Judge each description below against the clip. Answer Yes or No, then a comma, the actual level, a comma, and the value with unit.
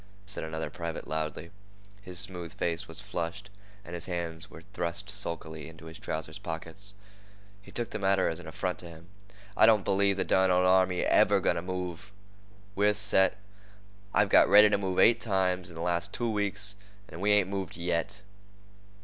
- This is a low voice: Yes, very low, 90 Hz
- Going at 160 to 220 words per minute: Yes, average, 185 wpm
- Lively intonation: No, average, 3.1 semitones